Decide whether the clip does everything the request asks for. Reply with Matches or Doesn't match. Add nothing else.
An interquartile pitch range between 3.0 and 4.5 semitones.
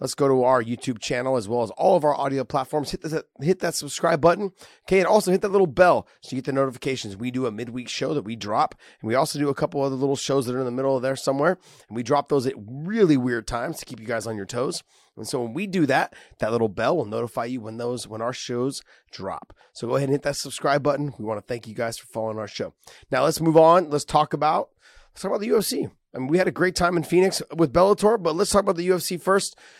Doesn't match